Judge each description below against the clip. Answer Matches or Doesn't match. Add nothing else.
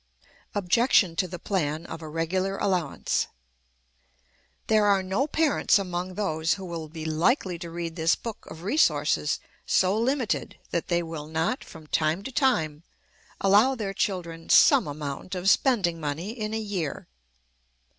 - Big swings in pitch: Doesn't match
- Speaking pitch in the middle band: Matches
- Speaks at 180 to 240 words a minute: Doesn't match